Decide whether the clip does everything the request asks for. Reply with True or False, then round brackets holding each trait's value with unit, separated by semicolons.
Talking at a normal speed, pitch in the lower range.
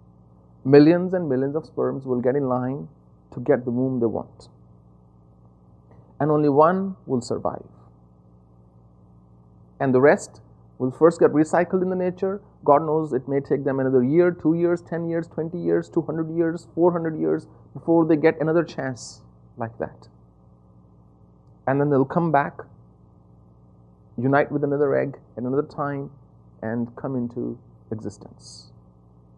True (150 wpm; 125 Hz)